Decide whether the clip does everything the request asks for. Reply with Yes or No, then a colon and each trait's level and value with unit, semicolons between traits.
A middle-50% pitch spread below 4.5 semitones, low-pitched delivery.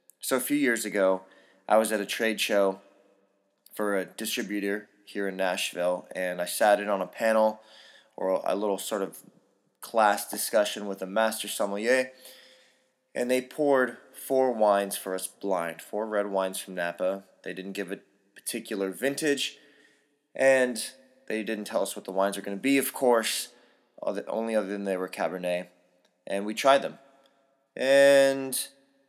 No: average, 4.9 semitones; low, 105 Hz